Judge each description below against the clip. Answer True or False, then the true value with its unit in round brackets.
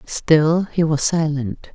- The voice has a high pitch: False (155 Hz)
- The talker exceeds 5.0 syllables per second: False (3.1 syllables/s)